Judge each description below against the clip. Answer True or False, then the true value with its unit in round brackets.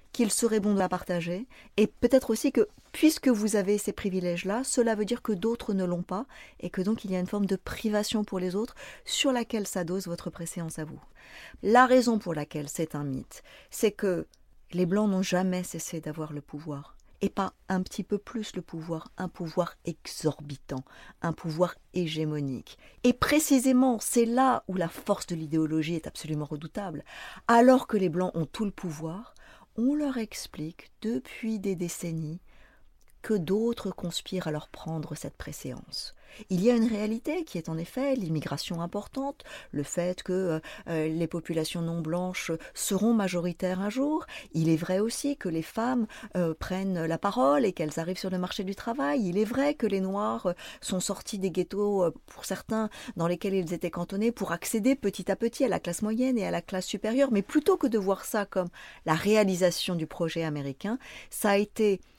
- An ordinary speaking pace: True (190 wpm)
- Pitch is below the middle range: False (190 Hz)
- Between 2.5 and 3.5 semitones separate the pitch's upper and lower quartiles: False (4.7 semitones)